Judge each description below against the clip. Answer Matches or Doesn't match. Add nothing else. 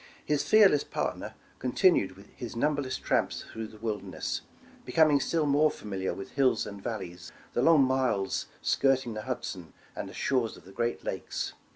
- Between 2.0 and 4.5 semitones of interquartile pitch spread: Doesn't match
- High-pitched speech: Doesn't match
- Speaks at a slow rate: Doesn't match